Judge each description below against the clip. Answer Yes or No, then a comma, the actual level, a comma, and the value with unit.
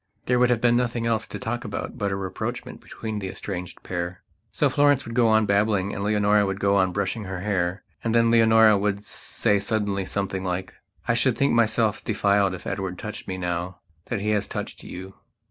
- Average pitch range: Yes, average, 3.1 semitones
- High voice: No, low, 105 Hz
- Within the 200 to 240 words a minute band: Yes, fast, 205 wpm